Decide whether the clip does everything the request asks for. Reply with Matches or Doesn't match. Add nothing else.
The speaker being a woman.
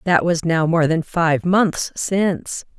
Matches